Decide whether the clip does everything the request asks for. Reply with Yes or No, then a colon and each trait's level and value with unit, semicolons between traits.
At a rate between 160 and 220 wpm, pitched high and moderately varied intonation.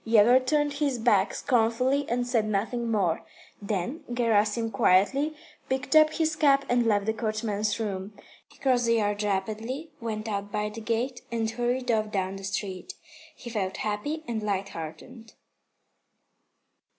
No: average, 150 wpm; high, 225 Hz; average, 3.4 semitones